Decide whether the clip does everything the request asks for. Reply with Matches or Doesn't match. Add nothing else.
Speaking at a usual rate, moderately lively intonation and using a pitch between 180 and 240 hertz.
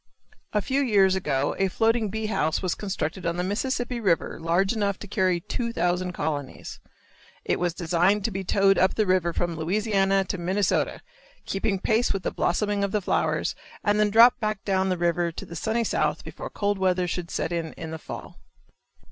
Matches